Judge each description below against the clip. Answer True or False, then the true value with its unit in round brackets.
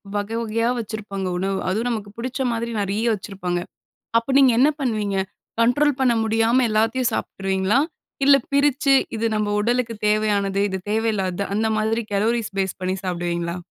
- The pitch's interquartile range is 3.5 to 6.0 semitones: False (3.1 semitones)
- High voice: True (215 Hz)